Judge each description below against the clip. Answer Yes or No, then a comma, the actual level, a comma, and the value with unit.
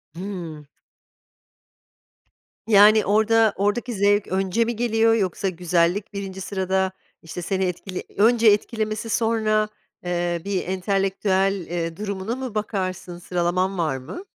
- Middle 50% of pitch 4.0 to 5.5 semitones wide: No, average, 2.9 semitones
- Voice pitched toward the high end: Yes, high, 195 Hz